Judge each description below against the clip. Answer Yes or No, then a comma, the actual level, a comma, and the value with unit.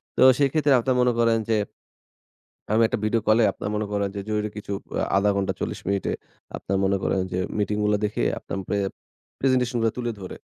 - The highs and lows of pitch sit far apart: No, average, 2.9 semitones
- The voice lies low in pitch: Yes, low, 105 Hz